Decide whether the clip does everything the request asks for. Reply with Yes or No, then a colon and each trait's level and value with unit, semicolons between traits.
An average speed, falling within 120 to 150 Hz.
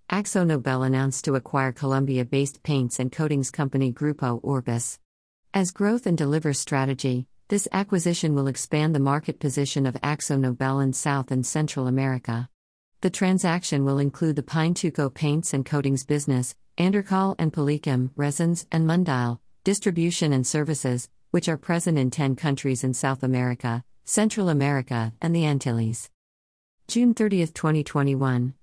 Yes: average, 145 wpm; medium, 140 Hz